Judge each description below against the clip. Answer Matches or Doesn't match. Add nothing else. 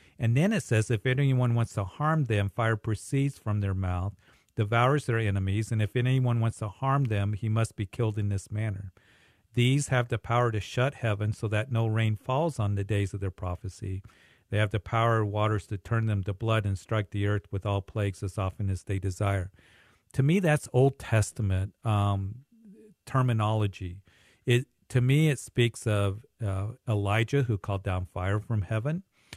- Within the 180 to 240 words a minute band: Matches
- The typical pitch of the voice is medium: Doesn't match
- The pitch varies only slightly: Doesn't match